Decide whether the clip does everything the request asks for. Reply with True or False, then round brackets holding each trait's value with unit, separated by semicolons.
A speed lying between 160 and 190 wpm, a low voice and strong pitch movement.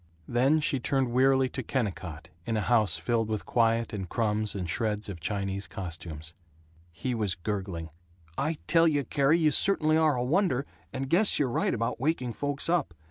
True (180 wpm; 120 Hz; 5.9 semitones)